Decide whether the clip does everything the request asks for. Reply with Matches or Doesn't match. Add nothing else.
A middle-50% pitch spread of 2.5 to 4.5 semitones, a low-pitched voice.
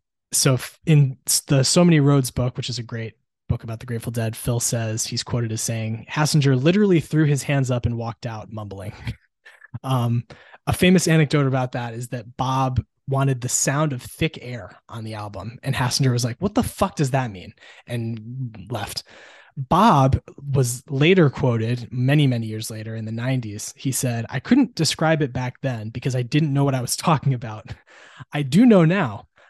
Matches